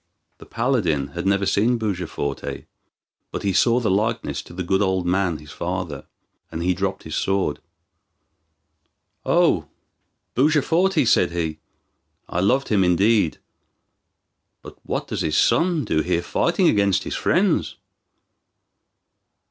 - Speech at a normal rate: No, slow, 130 wpm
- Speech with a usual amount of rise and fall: Yes, average, 4.6 semitones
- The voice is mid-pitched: No, very low, 95 Hz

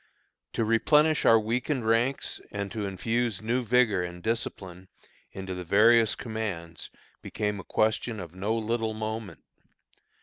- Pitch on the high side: No, low, 110 Hz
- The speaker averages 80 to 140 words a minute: Yes, slow, 135 wpm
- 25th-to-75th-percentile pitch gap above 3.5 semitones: No, average, 2.9 semitones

